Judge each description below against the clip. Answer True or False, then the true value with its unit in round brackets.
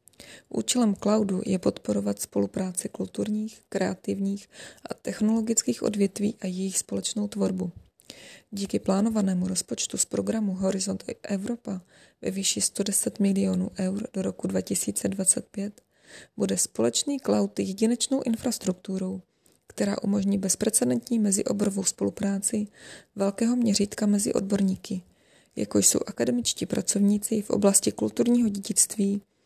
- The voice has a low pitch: False (200 Hz)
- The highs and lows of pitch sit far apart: False (2.4 semitones)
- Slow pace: True (105 wpm)